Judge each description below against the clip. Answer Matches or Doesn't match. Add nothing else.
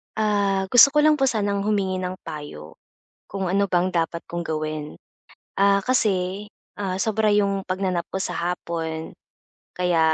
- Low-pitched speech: Doesn't match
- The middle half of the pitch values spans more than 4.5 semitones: Doesn't match